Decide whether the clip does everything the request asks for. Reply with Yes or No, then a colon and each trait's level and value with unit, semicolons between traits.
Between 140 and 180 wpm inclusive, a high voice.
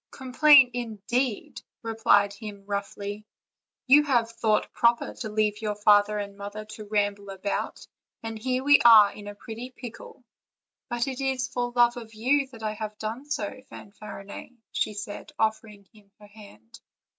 Yes: average, 160 wpm; high, 215 Hz